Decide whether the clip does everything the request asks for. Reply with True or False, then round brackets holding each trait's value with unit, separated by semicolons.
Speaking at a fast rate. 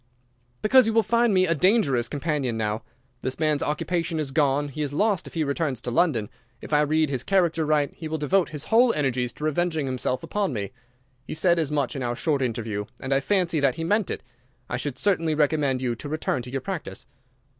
True (220 wpm)